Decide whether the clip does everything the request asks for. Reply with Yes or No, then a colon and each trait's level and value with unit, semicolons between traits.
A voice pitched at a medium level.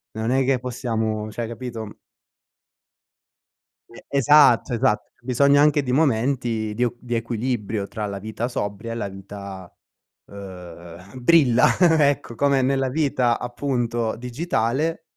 No: low, 120 Hz